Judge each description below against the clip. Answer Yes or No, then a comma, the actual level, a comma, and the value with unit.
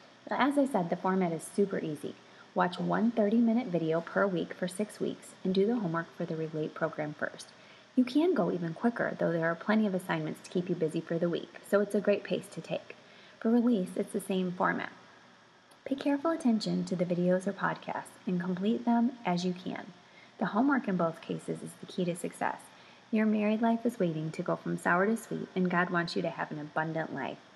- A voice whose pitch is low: No, high, 190 Hz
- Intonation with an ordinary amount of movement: Yes, average, 4.3 semitones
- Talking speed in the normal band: No, fast, 220 wpm